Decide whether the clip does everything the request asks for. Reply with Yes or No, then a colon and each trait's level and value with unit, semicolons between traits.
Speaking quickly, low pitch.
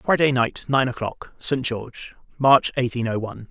No: average, 170 wpm; low, 125 Hz